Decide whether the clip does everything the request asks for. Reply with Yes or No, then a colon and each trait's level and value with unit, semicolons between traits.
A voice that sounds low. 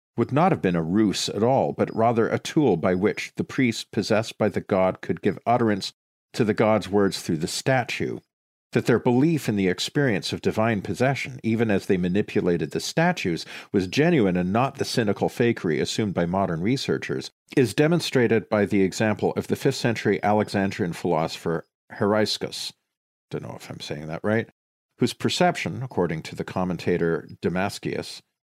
Yes: low, 105 Hz